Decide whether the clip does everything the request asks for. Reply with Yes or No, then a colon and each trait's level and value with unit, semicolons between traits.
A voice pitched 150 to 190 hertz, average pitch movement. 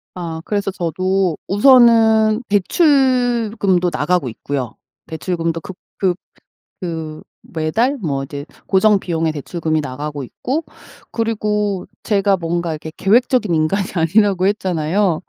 Yes: medium, 185 Hz; average, 4.8 semitones